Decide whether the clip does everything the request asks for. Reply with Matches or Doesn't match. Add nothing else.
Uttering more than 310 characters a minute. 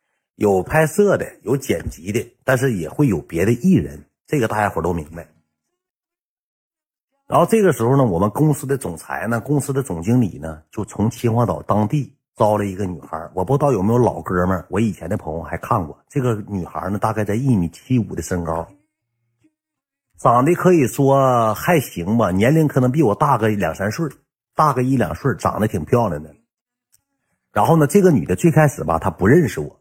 Doesn't match